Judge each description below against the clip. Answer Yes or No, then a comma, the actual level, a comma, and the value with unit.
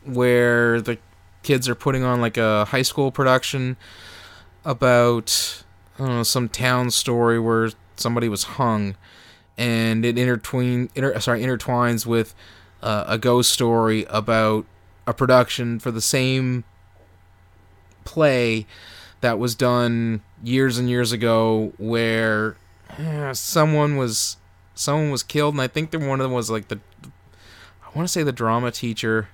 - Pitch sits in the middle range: No, low, 115 Hz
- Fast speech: No, average, 145 wpm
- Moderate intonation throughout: Yes, average, 3.6 semitones